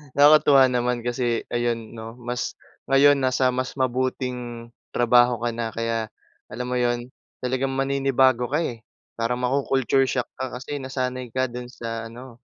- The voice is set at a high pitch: No, low, 125 Hz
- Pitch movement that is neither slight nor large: No, narrow, 1.7 semitones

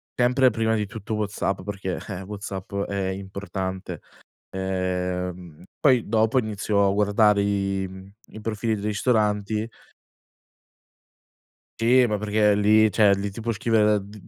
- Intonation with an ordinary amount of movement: No, narrow, 2.0 semitones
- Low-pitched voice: Yes, low, 105 Hz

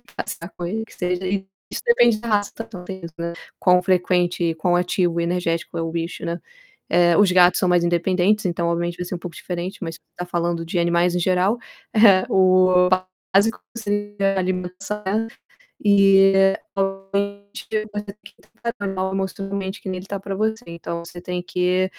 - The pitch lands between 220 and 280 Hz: No, medium, 185 Hz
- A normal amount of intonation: No, narrow, 2.2 semitones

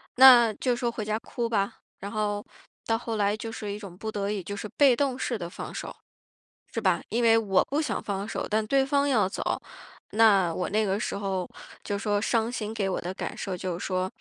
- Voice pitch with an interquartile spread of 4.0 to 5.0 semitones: No, average, 2.8 semitones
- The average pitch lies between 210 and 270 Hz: Yes, high, 215 Hz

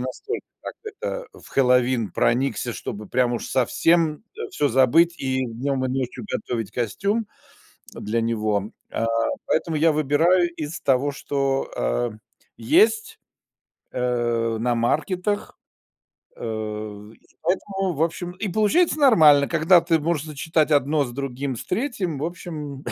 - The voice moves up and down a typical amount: No, wide, 6.0 semitones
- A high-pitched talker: No, medium, 140 Hz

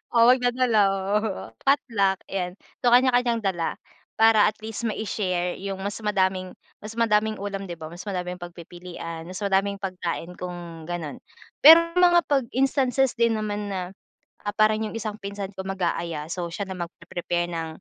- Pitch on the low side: No, high, 200 Hz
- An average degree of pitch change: Yes, average, 3.9 semitones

